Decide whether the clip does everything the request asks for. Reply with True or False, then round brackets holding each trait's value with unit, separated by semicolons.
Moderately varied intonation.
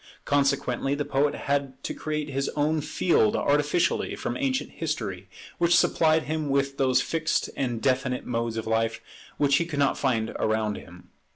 True (4.1 semitones)